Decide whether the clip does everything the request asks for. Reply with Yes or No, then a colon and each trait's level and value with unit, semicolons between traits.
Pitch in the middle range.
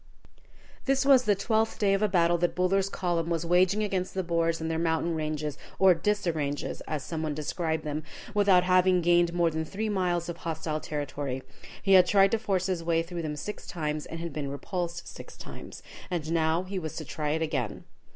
Yes: medium, 170 Hz